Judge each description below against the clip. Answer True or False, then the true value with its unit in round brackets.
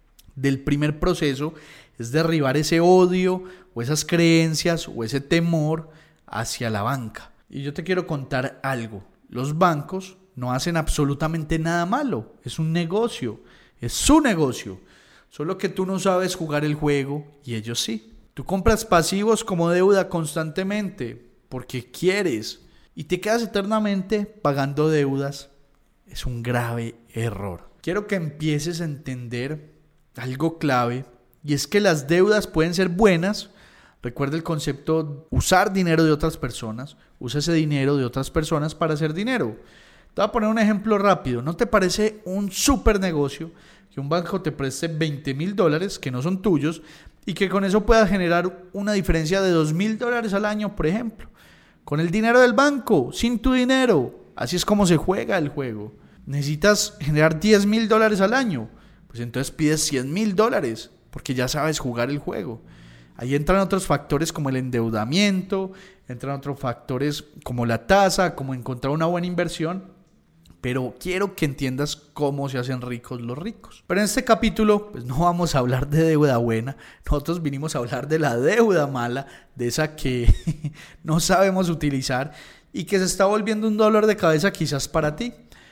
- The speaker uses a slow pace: False (165 wpm)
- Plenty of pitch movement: True (5.8 semitones)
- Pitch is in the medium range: True (160 Hz)